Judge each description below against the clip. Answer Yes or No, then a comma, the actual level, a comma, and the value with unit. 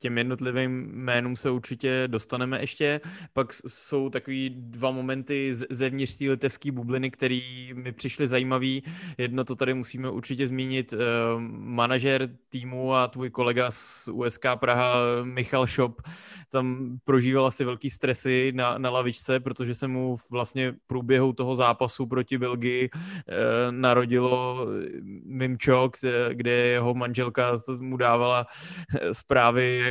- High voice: No, low, 130 Hz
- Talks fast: No, average, 130 wpm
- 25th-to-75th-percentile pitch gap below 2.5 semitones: Yes, narrow, 1.2 semitones